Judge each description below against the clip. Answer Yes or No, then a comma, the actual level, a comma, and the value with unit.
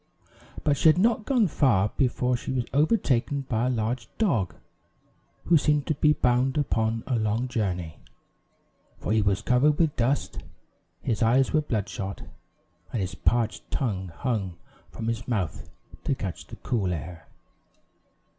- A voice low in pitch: Yes, low, 120 Hz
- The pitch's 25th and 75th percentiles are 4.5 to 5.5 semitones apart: Yes, average, 5.0 semitones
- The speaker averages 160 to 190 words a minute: No, average, 150 wpm